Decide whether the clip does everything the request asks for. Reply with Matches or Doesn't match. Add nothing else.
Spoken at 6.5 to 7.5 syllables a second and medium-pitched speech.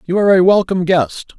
Matches